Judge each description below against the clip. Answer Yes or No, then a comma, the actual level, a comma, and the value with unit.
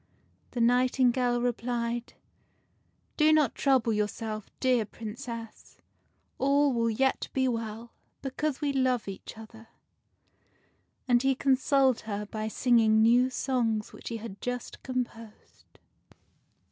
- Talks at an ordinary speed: No, slow, 120 wpm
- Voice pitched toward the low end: No, high, 240 Hz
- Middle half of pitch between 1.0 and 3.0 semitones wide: Yes, narrow, 2.6 semitones